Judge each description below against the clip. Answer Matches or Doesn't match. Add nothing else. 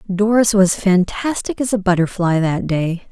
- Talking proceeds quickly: Doesn't match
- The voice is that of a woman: Matches